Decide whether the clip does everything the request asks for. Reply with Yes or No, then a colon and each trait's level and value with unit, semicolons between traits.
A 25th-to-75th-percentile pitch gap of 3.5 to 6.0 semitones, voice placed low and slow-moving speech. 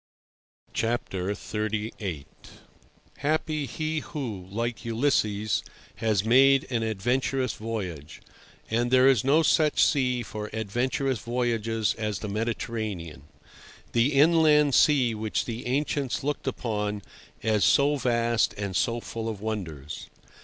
Yes: average, 4.0 semitones; low, 115 Hz; slow, 110 wpm